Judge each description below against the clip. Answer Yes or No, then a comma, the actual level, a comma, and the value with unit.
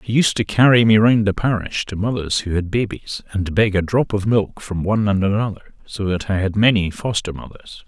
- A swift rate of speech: Yes, fast, 230 wpm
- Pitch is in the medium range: No, low, 100 Hz